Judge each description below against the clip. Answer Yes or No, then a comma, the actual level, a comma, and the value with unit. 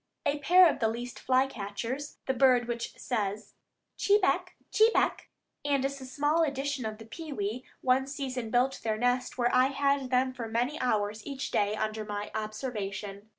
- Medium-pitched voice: No, very high, 250 Hz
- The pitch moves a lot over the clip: No, average, 4.0 semitones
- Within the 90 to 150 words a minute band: No, average, 170 wpm